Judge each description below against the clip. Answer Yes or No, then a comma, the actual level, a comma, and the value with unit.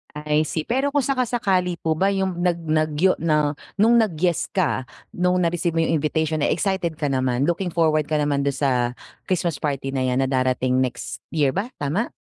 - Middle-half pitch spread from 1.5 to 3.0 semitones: No, average, 4.1 semitones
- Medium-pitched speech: Yes, medium, 160 Hz